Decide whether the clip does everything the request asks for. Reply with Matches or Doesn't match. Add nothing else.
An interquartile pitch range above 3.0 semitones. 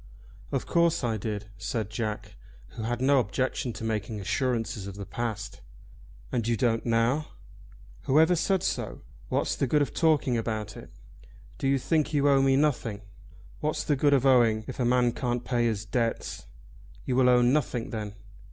Matches